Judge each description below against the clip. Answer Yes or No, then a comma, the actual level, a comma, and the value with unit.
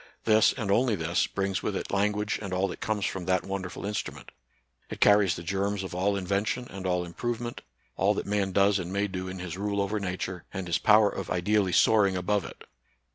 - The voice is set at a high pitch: No, low, 100 Hz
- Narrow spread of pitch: Yes, narrow, 2.0 semitones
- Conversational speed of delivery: No, fast, 210 wpm